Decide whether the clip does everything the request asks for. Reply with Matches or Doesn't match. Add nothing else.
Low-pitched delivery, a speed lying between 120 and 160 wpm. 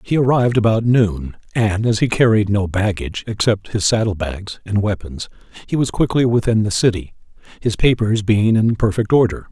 Doesn't match